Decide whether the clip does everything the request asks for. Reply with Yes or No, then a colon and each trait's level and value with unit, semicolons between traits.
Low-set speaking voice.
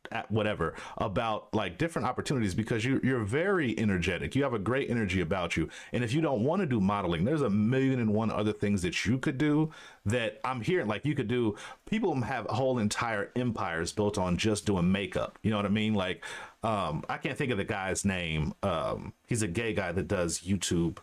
Yes: low, 105 Hz